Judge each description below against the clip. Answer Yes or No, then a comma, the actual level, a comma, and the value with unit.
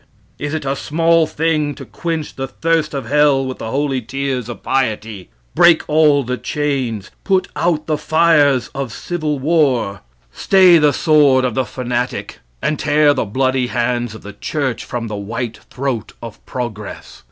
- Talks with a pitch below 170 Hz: Yes, low, 135 Hz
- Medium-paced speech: Yes, average, 165 wpm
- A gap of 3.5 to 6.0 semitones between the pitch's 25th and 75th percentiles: Yes, average, 4.0 semitones